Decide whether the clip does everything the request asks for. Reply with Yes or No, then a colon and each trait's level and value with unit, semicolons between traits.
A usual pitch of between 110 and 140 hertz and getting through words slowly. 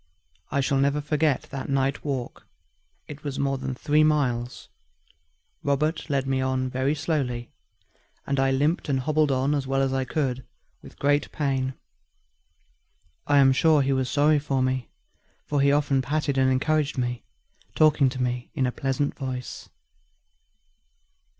No: low, 135 Hz; average, 155 wpm